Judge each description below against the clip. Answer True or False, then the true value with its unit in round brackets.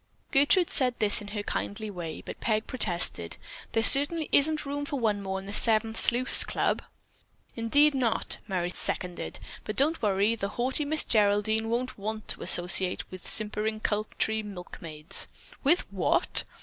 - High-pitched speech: True (220 Hz)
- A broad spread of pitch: False (4.3 semitones)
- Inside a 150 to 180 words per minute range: True (155 wpm)